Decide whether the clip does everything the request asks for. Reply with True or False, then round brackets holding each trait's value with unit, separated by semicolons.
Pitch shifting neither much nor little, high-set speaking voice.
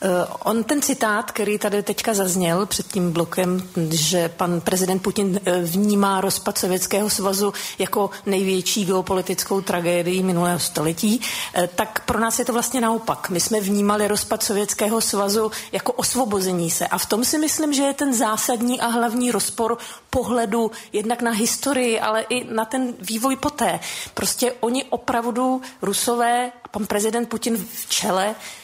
True (3.6 semitones; 215 Hz)